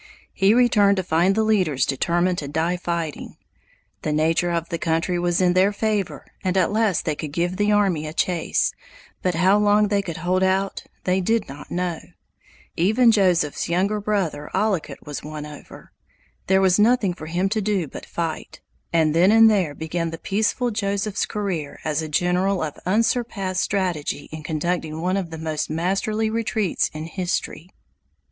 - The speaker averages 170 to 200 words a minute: Yes, average, 175 wpm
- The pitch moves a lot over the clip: No, average, 3.8 semitones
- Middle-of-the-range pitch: Yes, medium, 180 Hz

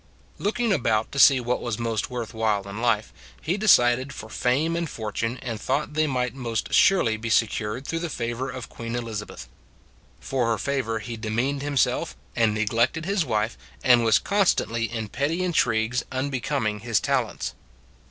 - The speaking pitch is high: No, low, 120 Hz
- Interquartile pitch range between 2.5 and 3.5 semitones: No, average, 3.9 semitones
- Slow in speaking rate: No, average, 170 wpm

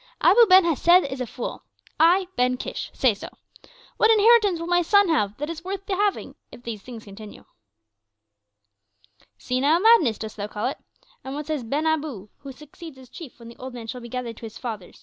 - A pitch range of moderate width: No, wide, 6.9 semitones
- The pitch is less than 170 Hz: No, very high, 275 Hz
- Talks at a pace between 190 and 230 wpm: Yes, fast, 205 wpm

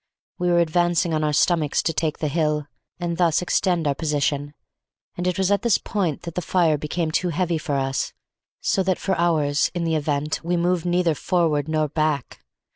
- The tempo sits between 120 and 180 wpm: No, average, 200 wpm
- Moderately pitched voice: Yes, medium, 165 Hz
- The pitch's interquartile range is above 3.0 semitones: No, average, 2.7 semitones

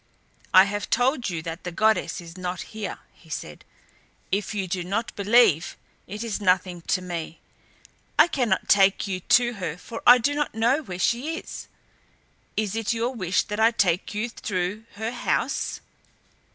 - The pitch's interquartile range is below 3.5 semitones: No, average, 4.1 semitones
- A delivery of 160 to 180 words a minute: Yes, average, 170 wpm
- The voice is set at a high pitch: Yes, high, 205 Hz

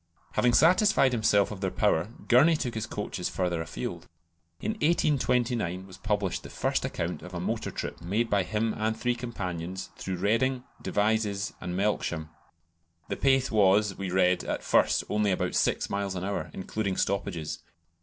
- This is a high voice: No, low, 105 Hz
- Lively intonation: No, average, 4.0 semitones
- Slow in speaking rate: No, average, 165 wpm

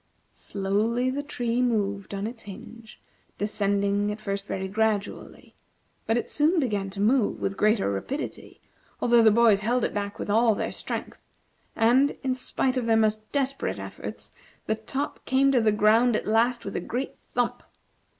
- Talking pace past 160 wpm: Yes, average, 170 wpm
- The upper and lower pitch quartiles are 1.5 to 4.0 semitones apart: Yes, average, 3.3 semitones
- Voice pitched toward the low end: No, high, 220 Hz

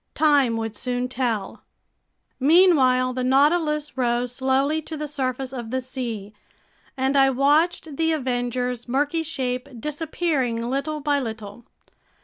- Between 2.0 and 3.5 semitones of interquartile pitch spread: Yes, average, 3.2 semitones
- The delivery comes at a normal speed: No, slow, 130 wpm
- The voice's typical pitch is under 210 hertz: No, very high, 265 Hz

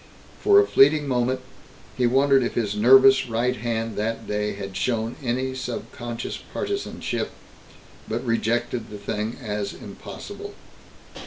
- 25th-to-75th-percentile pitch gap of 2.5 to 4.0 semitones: Yes, average, 2.9 semitones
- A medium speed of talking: No, slow, 130 wpm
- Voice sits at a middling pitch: No, low, 120 Hz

